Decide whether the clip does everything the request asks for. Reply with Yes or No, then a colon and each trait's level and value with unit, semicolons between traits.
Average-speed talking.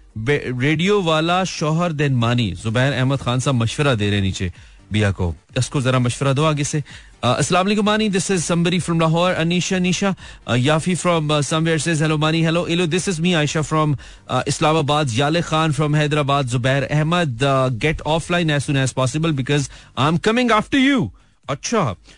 Yes: average, 160 wpm